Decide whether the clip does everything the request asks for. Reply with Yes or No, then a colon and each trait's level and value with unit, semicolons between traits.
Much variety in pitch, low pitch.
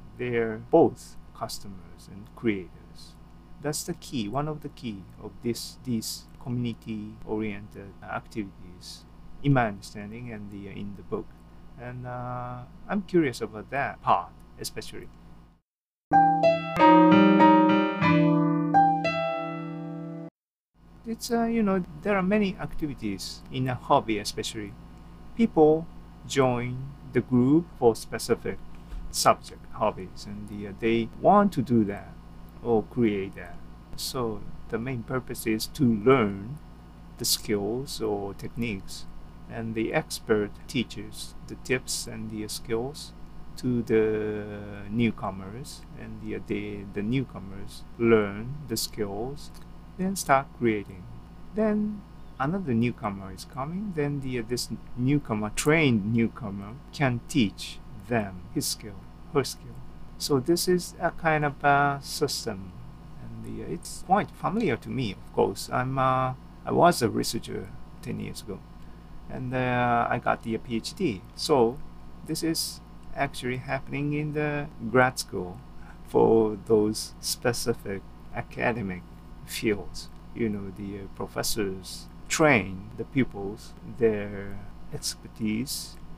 Yes: wide, 6.0 semitones; low, 120 Hz